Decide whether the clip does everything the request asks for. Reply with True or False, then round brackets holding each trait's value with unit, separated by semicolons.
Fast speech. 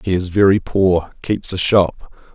False (180 wpm)